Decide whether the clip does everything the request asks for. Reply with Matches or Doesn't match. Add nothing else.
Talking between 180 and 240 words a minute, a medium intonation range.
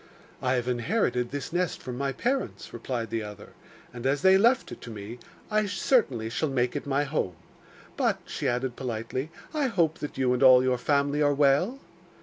Matches